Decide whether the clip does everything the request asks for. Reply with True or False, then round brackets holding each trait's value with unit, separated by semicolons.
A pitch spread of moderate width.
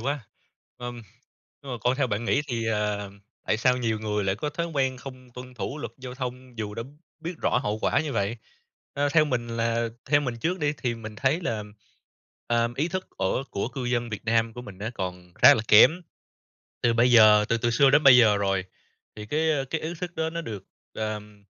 True (4.2 semitones)